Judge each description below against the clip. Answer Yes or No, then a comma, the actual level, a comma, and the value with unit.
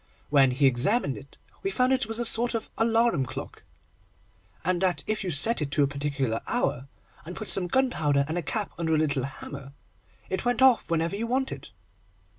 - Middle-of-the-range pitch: Yes, medium, 175 Hz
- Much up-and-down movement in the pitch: Yes, wide, 8.4 semitones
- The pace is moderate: Yes, average, 195 wpm